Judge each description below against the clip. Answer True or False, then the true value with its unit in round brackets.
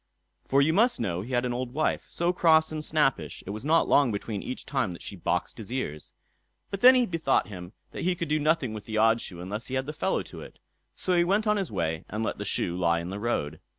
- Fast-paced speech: True (260 wpm)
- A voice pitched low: True (125 Hz)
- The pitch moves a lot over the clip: True (7.9 semitones)